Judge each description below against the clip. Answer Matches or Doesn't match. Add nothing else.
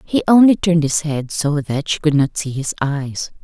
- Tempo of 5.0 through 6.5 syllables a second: Doesn't match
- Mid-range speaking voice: Matches